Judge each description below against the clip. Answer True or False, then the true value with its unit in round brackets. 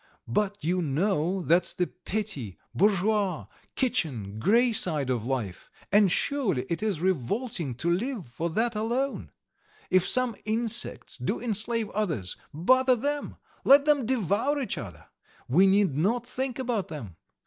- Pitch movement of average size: False (7.0 semitones)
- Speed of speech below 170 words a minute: True (140 wpm)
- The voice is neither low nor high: False (200 Hz)